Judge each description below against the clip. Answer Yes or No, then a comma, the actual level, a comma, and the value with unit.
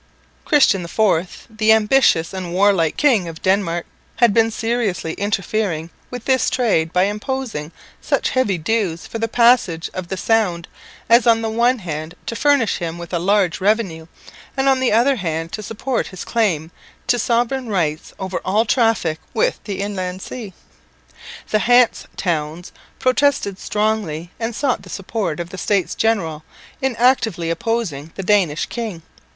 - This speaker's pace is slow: No, average, 155 wpm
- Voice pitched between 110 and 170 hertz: No, high, 205 Hz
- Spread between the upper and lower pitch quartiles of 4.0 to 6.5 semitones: Yes, average, 5.2 semitones